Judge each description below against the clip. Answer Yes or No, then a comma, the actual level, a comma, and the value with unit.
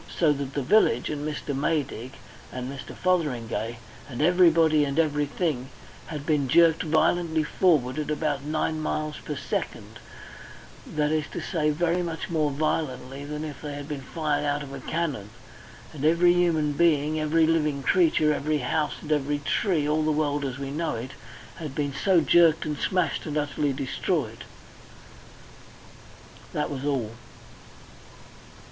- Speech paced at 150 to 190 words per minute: Yes, average, 155 wpm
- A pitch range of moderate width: No, narrow, 2.2 semitones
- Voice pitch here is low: No, medium, 150 Hz